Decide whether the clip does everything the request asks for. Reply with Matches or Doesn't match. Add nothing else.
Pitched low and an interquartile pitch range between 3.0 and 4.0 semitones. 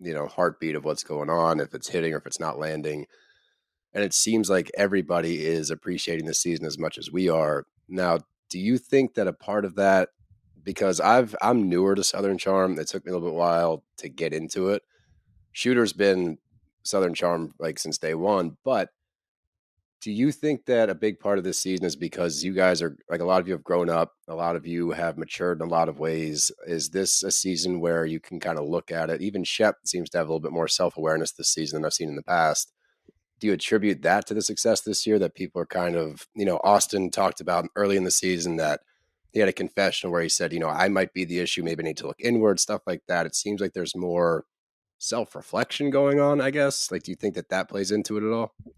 Matches